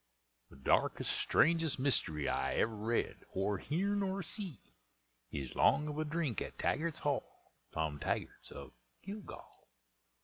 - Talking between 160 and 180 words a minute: No, slow, 135 wpm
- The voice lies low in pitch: No, medium, 150 Hz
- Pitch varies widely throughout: Yes, wide, 8.6 semitones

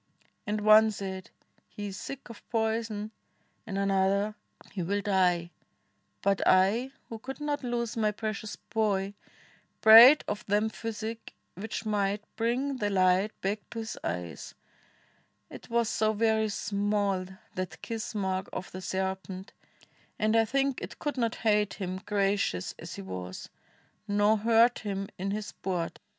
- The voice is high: Yes, high, 210 Hz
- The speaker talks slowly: No, average, 145 wpm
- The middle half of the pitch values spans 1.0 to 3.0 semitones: Yes, narrow, 2.6 semitones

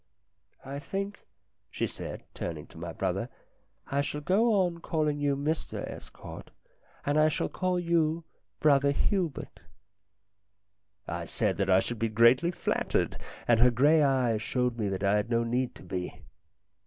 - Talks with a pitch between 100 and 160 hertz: Yes, medium, 140 Hz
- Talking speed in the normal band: Yes, average, 165 wpm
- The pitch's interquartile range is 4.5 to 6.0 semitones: Yes, wide, 5.5 semitones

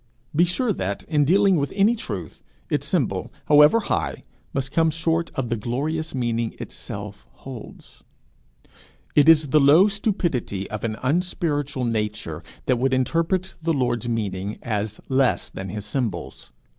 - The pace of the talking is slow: No, average, 145 wpm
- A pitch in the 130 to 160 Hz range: Yes, low, 135 Hz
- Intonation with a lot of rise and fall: Yes, wide, 7.1 semitones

